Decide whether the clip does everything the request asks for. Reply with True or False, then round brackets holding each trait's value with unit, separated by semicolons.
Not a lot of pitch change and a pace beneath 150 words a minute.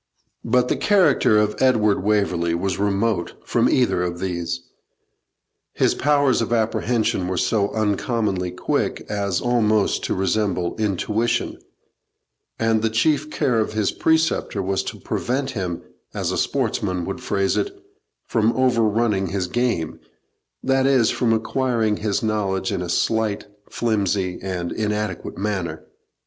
False (3.6 semitones; 135 wpm)